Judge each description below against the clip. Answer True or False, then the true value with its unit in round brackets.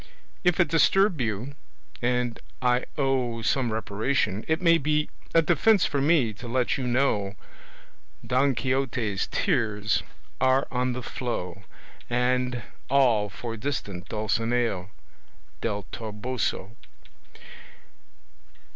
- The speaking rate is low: True (110 wpm)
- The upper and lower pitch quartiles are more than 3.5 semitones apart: True (4.0 semitones)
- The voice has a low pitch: True (125 Hz)